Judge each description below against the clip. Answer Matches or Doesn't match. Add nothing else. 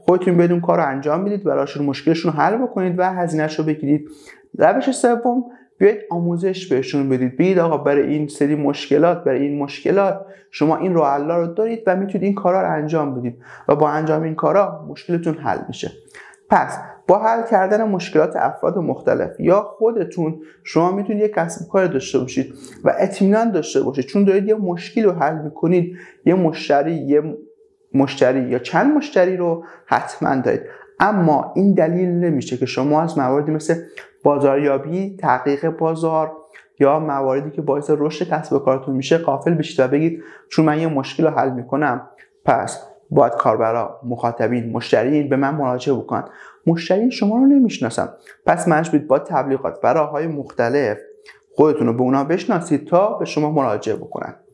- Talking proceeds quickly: Matches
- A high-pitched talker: Doesn't match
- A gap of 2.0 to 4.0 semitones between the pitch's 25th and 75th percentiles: Doesn't match